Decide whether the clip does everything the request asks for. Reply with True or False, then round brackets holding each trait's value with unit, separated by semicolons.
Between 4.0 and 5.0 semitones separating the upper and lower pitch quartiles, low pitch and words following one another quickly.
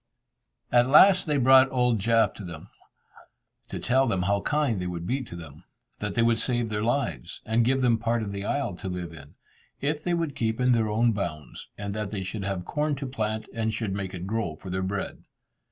True (4.7 semitones; 110 Hz; 220 wpm)